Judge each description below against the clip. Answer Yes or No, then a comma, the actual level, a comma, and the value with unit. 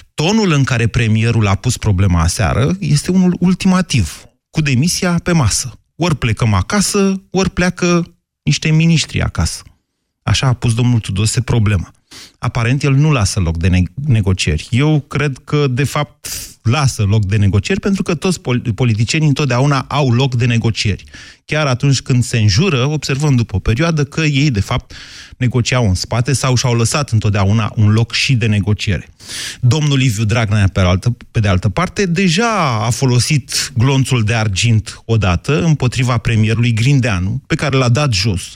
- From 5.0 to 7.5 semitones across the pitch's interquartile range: Yes, average, 5.3 semitones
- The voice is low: Yes, low, 125 Hz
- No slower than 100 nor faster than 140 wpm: No, average, 165 wpm